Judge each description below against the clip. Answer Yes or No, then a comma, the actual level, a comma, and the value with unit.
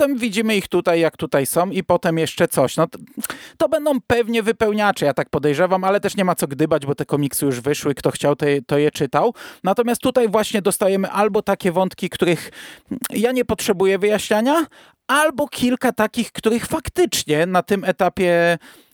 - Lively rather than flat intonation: Yes, wide, 6.4 semitones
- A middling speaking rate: No, fast, 180 wpm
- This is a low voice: No, high, 190 Hz